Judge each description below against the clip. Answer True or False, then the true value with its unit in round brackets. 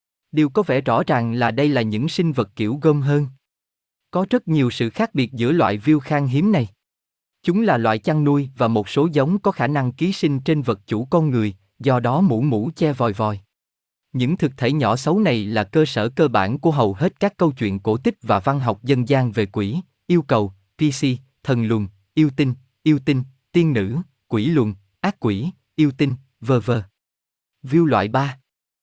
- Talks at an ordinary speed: True (205 wpm)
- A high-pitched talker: False (130 Hz)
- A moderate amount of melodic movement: False (6.0 semitones)